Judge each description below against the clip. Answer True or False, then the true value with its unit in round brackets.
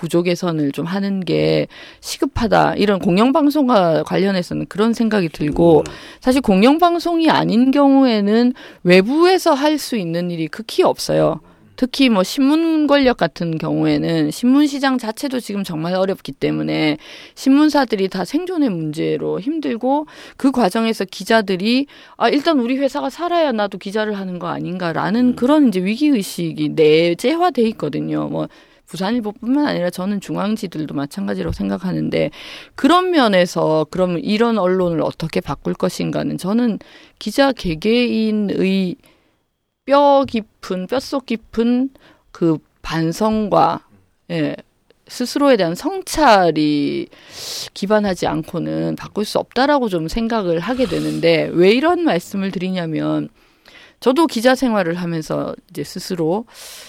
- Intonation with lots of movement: True (7.9 semitones)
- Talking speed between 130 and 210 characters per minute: False (295 characters per minute)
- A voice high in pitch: True (205 Hz)